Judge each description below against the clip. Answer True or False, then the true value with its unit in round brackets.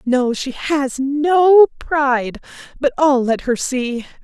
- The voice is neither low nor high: False (270 Hz)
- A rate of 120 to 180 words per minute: True (140 wpm)